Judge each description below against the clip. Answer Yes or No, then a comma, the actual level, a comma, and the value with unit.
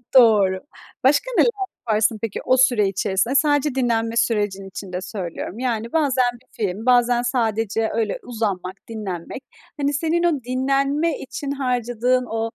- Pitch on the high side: Yes, high, 240 Hz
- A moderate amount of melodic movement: Yes, average, 3.8 semitones